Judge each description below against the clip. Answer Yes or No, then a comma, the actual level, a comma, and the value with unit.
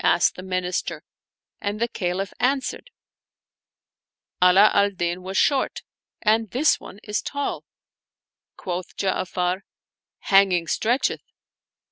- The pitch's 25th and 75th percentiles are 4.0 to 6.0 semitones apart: No, average, 3.4 semitones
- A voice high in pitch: Yes, high, 195 Hz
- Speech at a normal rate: No, slow, 115 wpm